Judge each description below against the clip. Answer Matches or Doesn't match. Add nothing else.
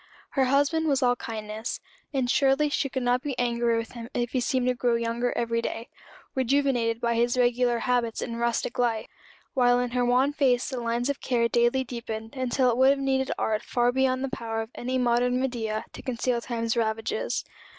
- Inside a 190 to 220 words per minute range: Matches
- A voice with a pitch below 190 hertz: Doesn't match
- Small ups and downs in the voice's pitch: Matches